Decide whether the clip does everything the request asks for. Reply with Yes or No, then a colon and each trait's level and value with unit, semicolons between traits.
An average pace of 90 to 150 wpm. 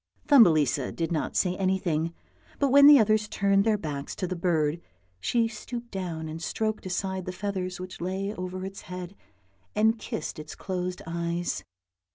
No: average, 165 wpm